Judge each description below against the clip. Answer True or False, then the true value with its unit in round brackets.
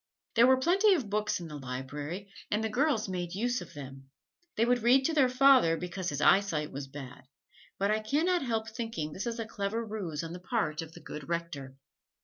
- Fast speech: True (210 wpm)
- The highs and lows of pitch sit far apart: True (7.5 semitones)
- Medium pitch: False (200 Hz)